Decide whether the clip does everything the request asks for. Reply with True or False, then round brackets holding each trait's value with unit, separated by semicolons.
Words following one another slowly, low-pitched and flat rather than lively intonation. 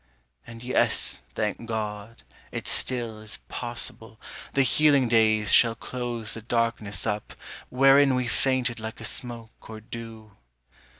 True (130 wpm; 115 Hz; 2.1 semitones)